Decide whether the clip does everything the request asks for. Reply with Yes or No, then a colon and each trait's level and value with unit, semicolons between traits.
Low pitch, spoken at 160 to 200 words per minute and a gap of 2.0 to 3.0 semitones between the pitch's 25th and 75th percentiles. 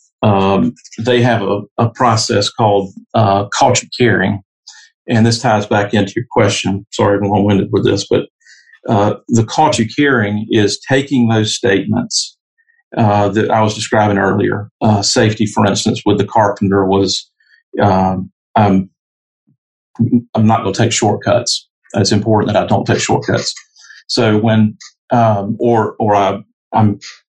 No: low, 105 Hz; average, 150 wpm; narrow, 2.5 semitones